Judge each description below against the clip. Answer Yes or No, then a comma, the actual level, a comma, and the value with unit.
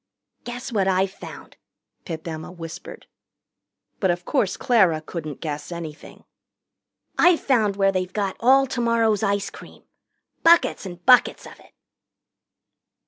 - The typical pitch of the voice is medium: No, high, 195 Hz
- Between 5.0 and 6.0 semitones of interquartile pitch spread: Yes, wide, 5.4 semitones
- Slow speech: Yes, slow, 130 wpm